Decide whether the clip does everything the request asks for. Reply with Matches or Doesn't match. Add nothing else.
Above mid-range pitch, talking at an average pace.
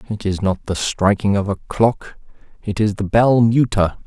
Doesn't match